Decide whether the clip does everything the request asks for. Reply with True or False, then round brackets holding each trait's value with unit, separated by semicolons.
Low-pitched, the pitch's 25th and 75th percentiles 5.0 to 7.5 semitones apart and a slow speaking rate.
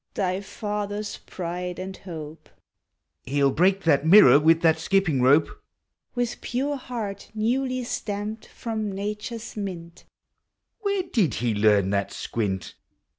False (195 Hz; 5.4 semitones; 130 wpm)